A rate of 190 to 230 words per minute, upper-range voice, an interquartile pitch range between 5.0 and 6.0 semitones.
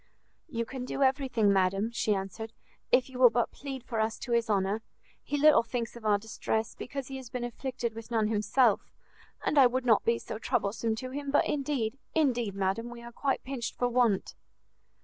No: average, 200 wpm; high, 235 Hz; average, 3.0 semitones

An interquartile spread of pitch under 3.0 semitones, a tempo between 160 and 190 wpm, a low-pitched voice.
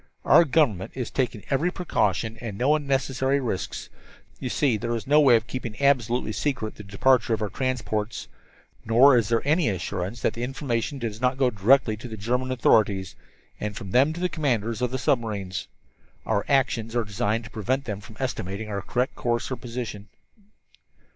No: average, 3.7 semitones; average, 180 wpm; low, 120 Hz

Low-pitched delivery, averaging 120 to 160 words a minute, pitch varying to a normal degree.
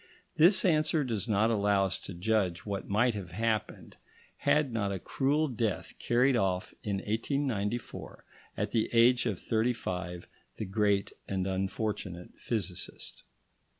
Yes: low, 110 Hz; average, 140 wpm; average, 3.8 semitones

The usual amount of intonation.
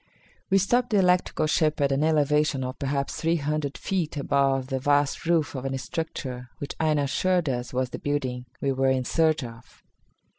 Yes: average, 3.1 semitones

